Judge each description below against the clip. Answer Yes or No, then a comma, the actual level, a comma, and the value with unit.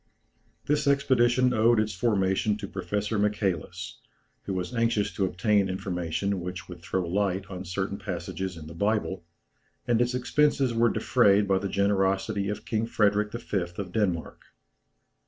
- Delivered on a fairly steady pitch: No, average, 3.0 semitones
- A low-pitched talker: Yes, low, 100 Hz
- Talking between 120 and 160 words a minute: Yes, average, 150 wpm